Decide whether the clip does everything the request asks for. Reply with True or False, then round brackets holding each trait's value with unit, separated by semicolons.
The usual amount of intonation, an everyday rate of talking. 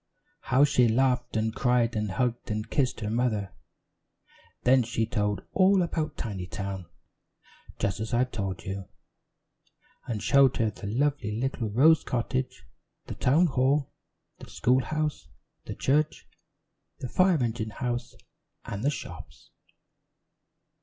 False (3.9 semitones; 130 wpm)